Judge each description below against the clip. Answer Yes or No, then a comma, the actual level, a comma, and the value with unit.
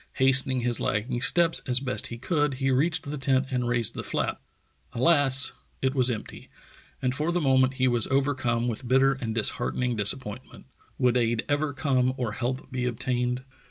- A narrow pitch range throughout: Yes, narrow, 1.9 semitones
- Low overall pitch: Yes, low, 130 Hz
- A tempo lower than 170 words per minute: No, average, 180 wpm